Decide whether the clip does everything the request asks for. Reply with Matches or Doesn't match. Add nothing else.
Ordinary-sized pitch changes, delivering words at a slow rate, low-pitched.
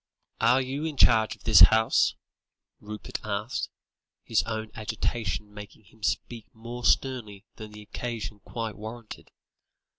Doesn't match